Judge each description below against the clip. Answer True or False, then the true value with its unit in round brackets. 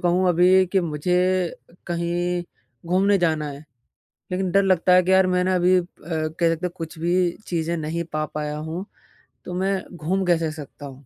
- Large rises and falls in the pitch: False (2.4 semitones)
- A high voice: False (175 Hz)